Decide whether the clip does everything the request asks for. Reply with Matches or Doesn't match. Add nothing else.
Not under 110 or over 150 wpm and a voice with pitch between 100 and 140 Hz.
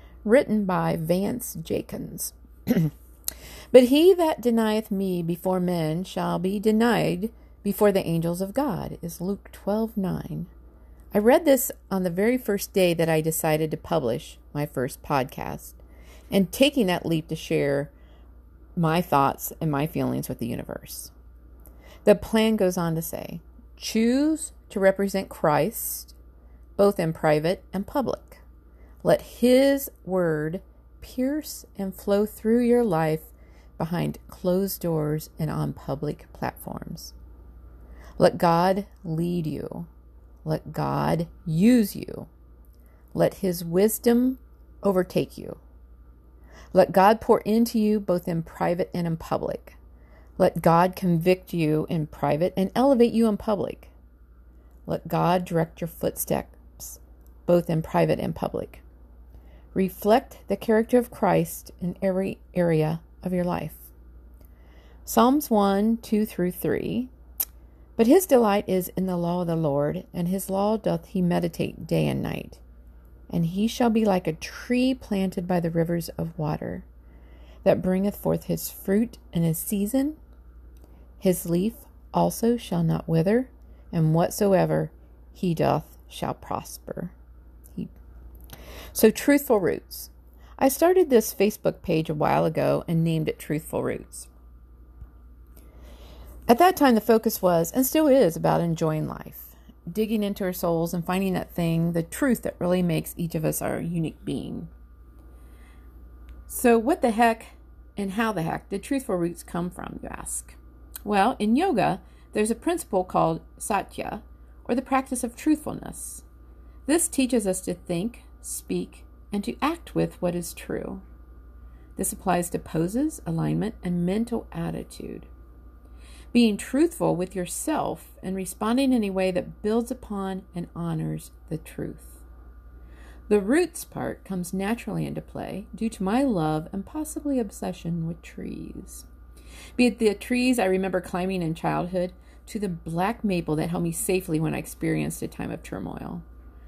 Doesn't match